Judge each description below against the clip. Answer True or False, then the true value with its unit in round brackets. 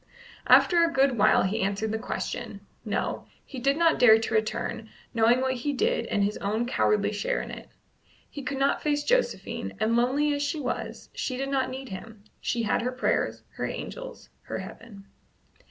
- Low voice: False (250 Hz)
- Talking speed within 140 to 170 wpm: False (185 wpm)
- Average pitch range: True (4.5 semitones)